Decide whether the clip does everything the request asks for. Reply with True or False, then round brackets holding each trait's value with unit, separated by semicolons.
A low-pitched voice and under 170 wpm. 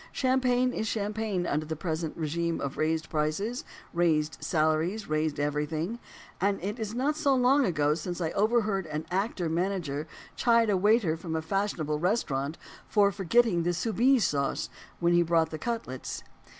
False (175 Hz; 155 wpm)